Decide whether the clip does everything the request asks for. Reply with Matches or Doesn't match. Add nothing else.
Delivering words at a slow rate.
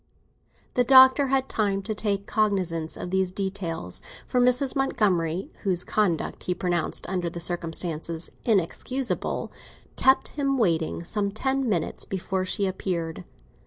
Matches